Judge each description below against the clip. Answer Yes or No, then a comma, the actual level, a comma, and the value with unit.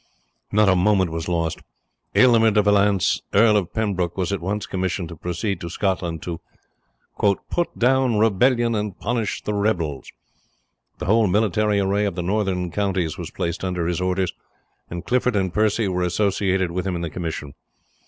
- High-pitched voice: No, very low, 95 Hz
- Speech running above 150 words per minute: Yes, average, 170 wpm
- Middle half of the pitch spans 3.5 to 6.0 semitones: No, average, 3.1 semitones